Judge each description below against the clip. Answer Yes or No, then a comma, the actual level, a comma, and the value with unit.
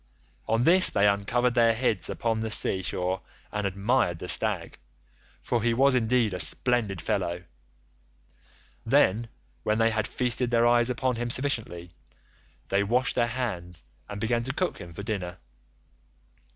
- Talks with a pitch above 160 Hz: No, low, 115 Hz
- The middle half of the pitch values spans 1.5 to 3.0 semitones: No, average, 3.7 semitones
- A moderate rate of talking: Yes, average, 150 wpm